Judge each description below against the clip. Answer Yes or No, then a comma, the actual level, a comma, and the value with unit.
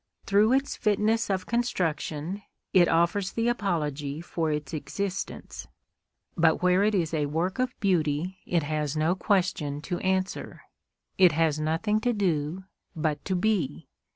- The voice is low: No, medium, 180 Hz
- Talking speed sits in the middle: Yes, average, 145 wpm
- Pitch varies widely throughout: No, average, 4.5 semitones